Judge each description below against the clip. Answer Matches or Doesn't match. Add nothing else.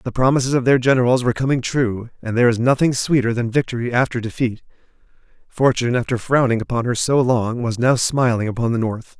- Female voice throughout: Doesn't match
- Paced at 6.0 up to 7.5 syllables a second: Matches